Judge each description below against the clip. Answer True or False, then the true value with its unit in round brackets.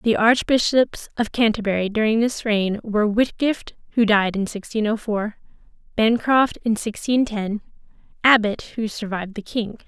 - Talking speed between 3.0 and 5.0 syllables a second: True (4.7 syllables/s)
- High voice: True (220 Hz)